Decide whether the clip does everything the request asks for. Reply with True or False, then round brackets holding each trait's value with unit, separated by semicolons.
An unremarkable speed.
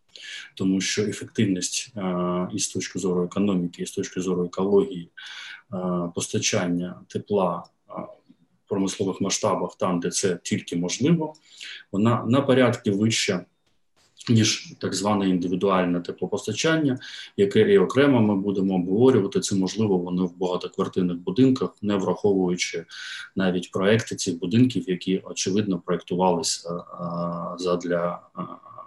True (115 wpm)